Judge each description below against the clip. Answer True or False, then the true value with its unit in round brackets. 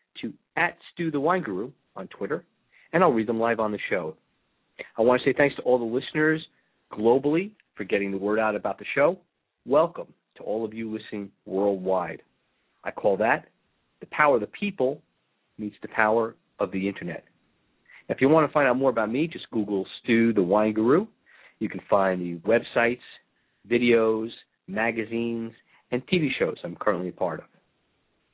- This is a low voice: True (115 Hz)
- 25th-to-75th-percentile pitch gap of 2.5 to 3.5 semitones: True (3.1 semitones)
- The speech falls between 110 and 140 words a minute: False (180 wpm)